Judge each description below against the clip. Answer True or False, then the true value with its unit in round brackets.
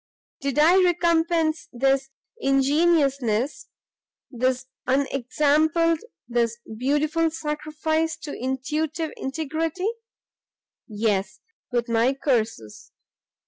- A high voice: True (280 Hz)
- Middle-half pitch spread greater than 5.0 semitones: False (4.0 semitones)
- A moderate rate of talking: False (75 wpm)